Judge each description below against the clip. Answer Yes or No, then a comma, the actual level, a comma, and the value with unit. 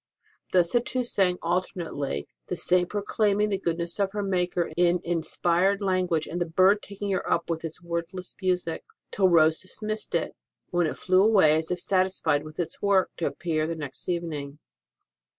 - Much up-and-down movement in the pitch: No, narrow, 2.6 semitones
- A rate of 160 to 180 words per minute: Yes, average, 175 wpm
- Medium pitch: Yes, medium, 180 Hz